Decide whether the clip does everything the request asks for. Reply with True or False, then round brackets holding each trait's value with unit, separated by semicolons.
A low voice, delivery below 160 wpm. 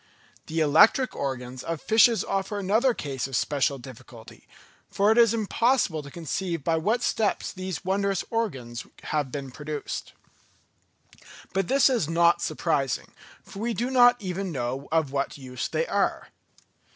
False (170 Hz; 150 wpm)